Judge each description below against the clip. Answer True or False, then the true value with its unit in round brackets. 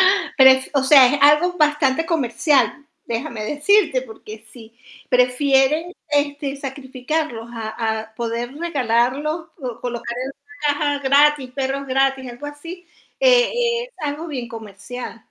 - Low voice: False (270 Hz)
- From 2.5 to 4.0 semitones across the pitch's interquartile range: True (3.7 semitones)